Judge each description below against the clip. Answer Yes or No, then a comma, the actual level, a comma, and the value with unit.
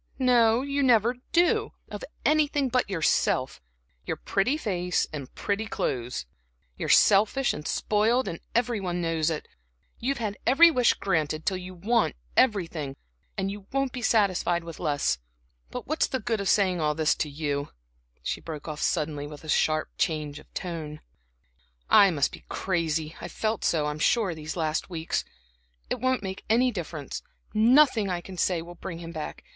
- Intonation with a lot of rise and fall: Yes, wide, 6.7 semitones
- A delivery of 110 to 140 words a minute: No, average, 165 wpm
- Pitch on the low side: No, medium, 185 Hz